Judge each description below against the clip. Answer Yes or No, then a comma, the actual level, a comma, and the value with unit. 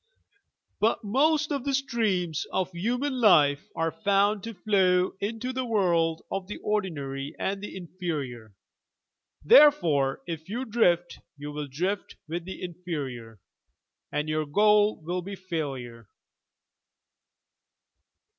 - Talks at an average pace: No, slow, 120 wpm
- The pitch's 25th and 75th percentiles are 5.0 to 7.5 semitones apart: Yes, wide, 5.6 semitones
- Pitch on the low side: No, medium, 180 Hz